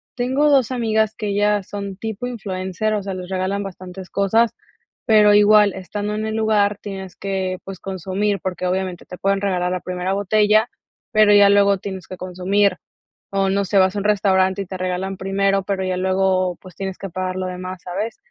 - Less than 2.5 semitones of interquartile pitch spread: Yes, narrow, 1.8 semitones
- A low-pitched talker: No, high, 195 Hz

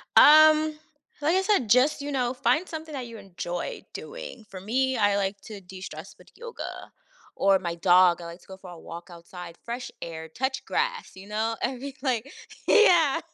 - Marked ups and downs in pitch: Yes, wide, 7.5 semitones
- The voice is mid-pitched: No, high, 230 Hz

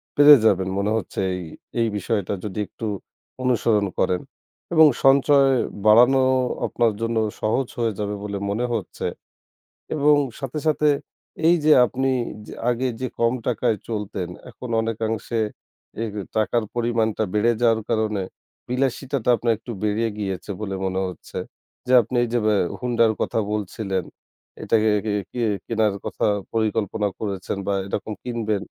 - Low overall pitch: Yes, low, 115 Hz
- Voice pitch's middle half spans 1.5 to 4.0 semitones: Yes, average, 2.8 semitones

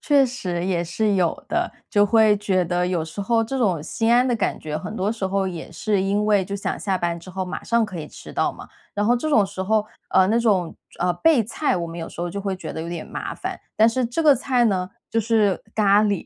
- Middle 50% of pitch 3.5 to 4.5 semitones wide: Yes, average, 3.9 semitones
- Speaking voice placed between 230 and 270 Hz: No, high, 200 Hz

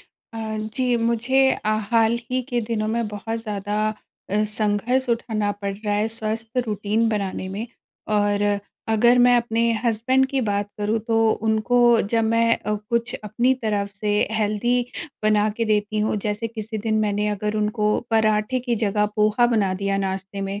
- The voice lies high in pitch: Yes, high, 215 Hz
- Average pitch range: No, narrow, 2.0 semitones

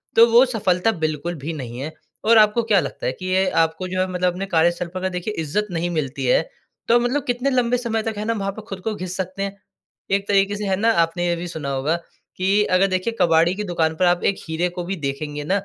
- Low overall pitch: No, medium, 185 Hz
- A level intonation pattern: No, average, 3.9 semitones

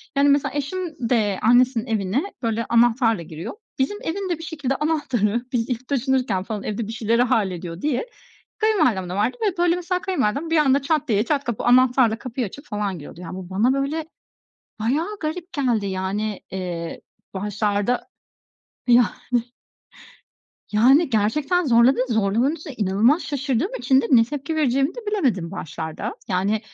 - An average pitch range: No, wide, 5.7 semitones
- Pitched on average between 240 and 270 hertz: Yes, high, 245 Hz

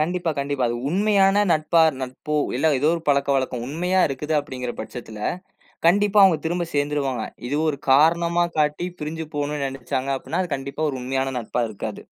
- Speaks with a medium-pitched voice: Yes, medium, 145 Hz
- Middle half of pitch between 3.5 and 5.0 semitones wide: Yes, average, 4.2 semitones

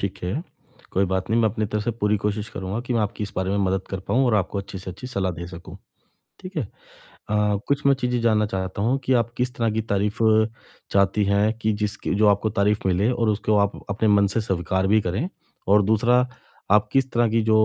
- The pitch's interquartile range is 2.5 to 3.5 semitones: Yes, average, 2.8 semitones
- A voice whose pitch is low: Yes, low, 105 Hz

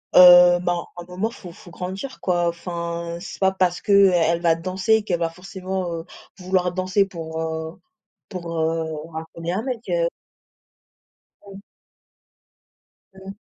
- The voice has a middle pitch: Yes, medium, 180 Hz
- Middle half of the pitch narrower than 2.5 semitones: Yes, narrow, 2.1 semitones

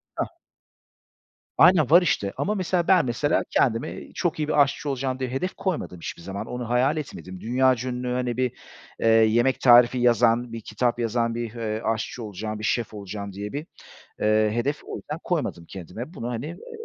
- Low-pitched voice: Yes, low, 120 Hz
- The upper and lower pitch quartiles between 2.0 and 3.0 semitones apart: No, average, 4.0 semitones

